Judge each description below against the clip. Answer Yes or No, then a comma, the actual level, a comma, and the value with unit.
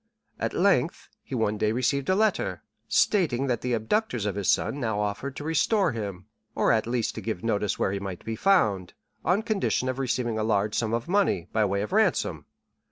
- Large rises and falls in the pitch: Yes, wide, 5.7 semitones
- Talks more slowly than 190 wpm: No, fast, 205 wpm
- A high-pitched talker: No, low, 115 Hz